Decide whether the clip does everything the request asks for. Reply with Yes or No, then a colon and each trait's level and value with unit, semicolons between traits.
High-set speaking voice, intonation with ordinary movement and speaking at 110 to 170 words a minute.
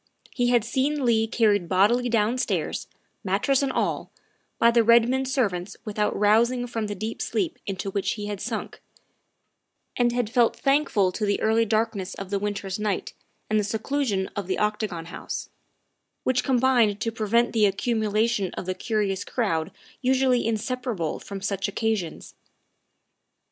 Yes: high, 220 Hz; average, 3.2 semitones; average, 160 wpm